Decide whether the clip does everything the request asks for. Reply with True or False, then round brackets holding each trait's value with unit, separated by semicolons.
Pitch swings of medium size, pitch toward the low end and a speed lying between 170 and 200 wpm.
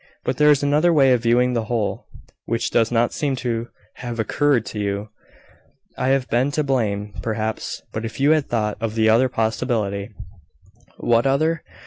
True (3.5 semitones; 120 Hz; 180 wpm)